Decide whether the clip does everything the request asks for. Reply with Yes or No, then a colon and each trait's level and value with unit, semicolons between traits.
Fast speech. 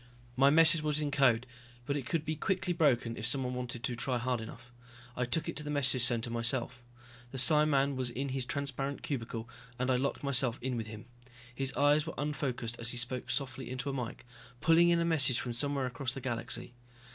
Yes: fast, 210 wpm